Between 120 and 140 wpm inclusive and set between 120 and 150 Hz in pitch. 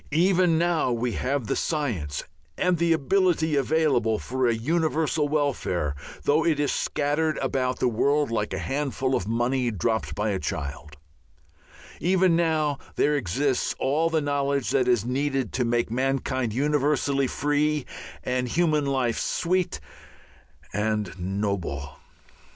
Yes: slow, 135 wpm; low, 135 Hz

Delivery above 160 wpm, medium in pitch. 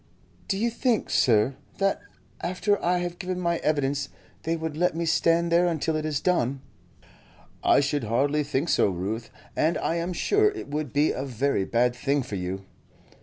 Yes: average, 180 wpm; medium, 155 Hz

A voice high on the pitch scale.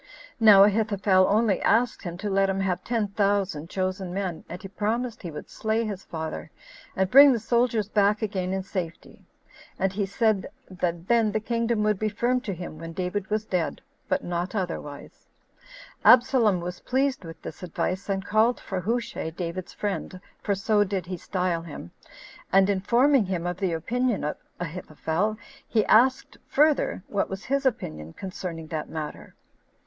Yes: high, 195 Hz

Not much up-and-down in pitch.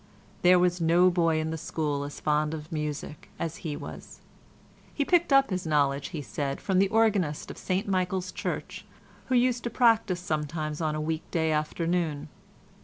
No: average, 3.4 semitones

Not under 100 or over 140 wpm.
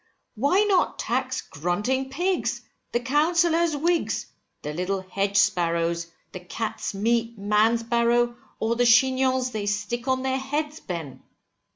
Yes: slow, 135 wpm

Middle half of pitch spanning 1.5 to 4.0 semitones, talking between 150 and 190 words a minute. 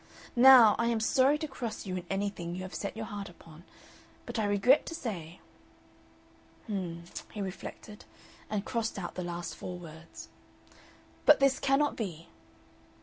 No: average, 4.9 semitones; average, 165 wpm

